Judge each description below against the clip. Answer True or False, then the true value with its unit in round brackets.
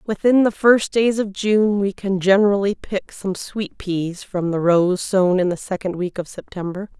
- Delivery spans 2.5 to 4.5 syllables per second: True (4.4 syllables/s)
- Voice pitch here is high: True (195 Hz)